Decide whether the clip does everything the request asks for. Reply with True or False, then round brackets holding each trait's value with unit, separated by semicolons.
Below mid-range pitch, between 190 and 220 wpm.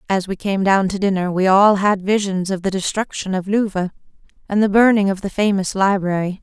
False (195 Hz; 205 wpm)